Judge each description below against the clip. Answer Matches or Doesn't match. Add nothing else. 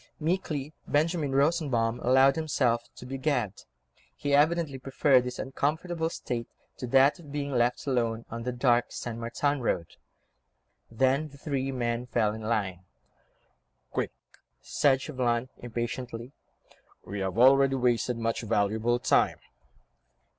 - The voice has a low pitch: Matches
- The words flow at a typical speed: Doesn't match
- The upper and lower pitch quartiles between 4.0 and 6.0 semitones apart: Doesn't match